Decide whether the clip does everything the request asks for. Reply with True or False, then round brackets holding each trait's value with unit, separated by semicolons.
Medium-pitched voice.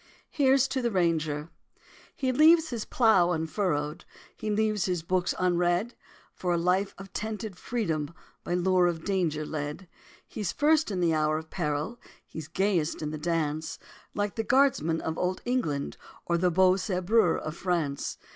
True (180 Hz)